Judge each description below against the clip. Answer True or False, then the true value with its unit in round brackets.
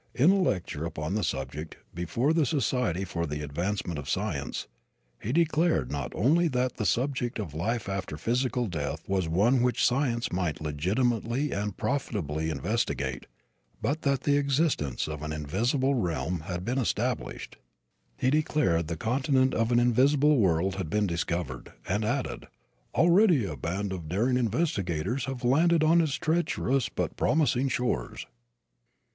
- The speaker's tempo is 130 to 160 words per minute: True (150 wpm)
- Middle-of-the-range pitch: False (115 Hz)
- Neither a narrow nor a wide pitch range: False (8.0 semitones)